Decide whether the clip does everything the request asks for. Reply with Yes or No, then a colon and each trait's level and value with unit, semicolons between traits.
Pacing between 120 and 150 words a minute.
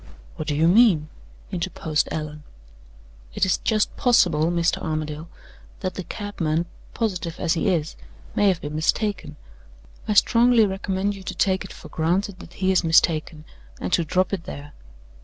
No: average, 160 wpm